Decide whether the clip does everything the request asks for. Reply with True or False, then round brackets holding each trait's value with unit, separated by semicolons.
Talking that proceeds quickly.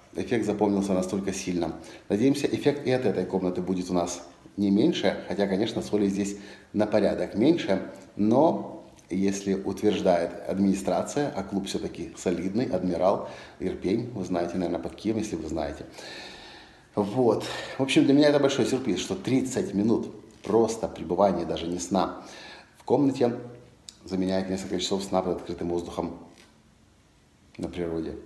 False (140 wpm)